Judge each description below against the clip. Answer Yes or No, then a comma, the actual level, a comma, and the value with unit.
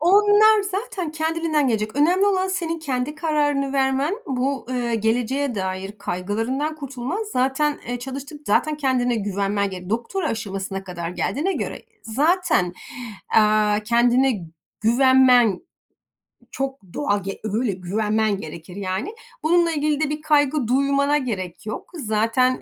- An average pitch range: No, wide, 6.0 semitones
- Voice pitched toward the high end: Yes, very high, 260 Hz